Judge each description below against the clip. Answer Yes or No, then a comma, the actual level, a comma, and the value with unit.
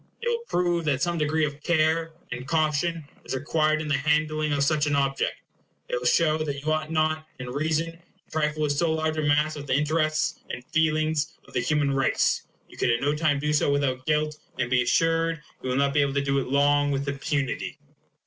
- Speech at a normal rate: No, fast, 220 wpm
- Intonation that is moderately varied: No, narrow, 2.0 semitones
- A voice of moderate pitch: Yes, medium, 150 Hz